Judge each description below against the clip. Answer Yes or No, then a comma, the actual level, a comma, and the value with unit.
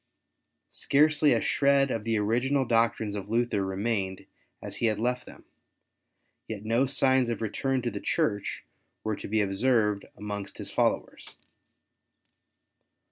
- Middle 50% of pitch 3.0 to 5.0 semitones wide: Yes, average, 3.9 semitones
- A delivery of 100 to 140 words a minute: Yes, slow, 135 wpm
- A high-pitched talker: No, low, 115 Hz